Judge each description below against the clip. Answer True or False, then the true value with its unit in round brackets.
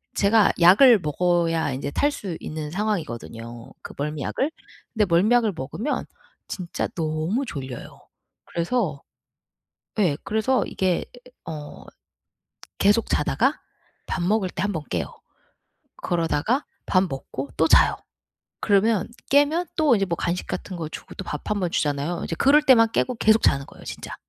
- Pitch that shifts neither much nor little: False (6.2 semitones)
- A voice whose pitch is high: False (180 Hz)